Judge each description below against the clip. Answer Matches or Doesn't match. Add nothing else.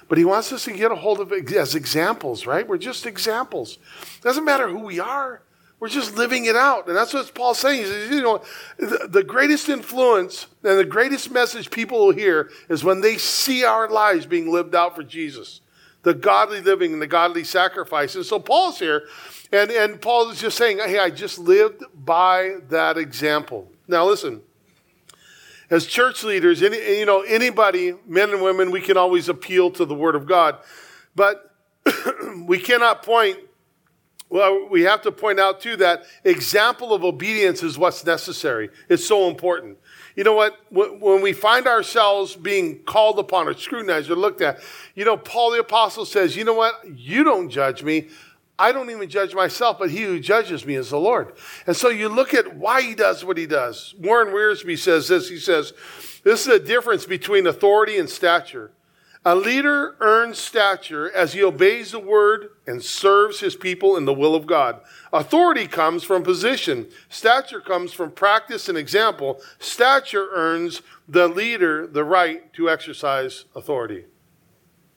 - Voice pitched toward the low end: Doesn't match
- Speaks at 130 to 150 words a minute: Doesn't match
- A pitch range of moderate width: Doesn't match